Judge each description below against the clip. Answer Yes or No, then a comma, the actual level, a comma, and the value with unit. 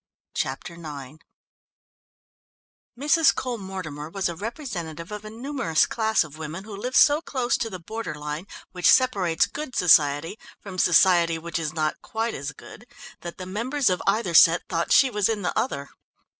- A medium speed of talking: Yes, average, 170 wpm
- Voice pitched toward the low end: No, medium, 185 Hz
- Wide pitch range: Yes, wide, 5.8 semitones